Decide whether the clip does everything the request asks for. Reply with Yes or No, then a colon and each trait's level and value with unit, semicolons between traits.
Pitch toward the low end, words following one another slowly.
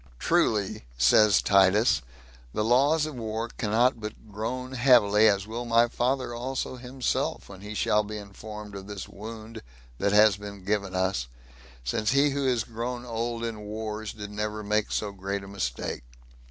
No: low, 110 Hz; average, 165 wpm